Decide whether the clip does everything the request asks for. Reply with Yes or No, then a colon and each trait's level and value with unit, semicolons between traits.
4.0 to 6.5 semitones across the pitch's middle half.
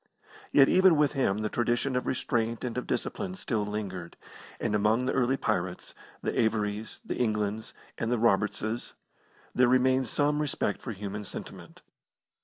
No: average, 3.6 semitones